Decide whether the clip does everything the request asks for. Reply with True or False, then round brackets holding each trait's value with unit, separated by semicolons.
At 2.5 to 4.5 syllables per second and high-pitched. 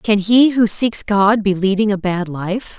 True (4.0 syllables/s; 205 Hz)